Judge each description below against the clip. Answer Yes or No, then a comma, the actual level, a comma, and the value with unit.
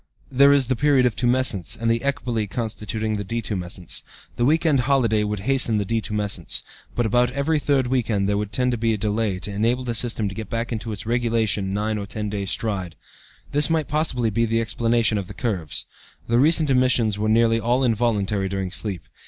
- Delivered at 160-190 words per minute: No, average, 200 wpm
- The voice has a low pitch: Yes, low, 115 Hz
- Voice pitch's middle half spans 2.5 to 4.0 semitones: Yes, average, 3.2 semitones